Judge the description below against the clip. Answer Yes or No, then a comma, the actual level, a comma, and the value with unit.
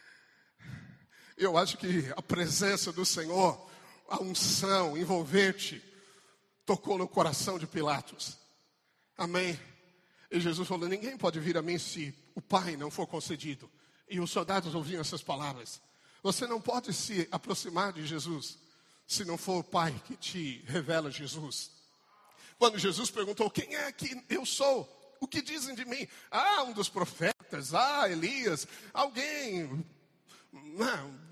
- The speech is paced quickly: No, average, 140 wpm